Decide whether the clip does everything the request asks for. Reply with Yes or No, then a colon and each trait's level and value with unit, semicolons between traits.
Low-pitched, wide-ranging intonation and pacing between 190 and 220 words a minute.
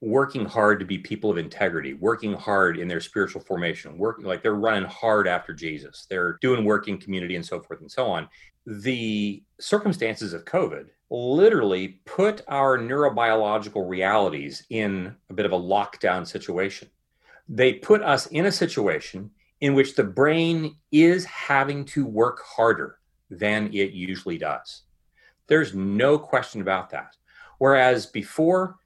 No: low, 110 Hz; wide, 6.2 semitones; average, 150 wpm